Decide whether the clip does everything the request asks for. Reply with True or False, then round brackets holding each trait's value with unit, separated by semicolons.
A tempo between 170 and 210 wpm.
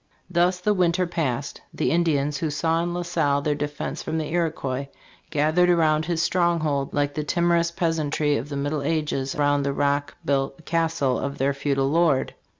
True (180 wpm)